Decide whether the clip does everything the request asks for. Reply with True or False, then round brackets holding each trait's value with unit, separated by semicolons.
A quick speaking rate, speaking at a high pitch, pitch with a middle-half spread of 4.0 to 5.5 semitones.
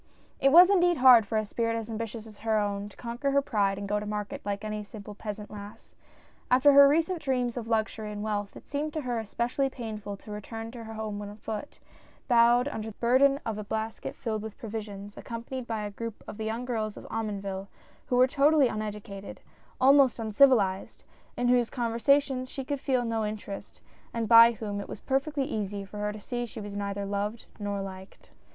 False (215 wpm; 225 Hz; 3.2 semitones)